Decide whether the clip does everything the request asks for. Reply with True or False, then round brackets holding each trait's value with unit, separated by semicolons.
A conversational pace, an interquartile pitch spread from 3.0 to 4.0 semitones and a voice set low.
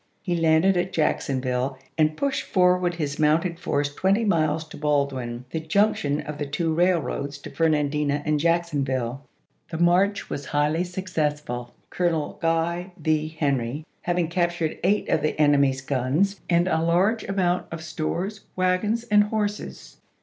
False (155 wpm; 3.7 semitones; 160 Hz)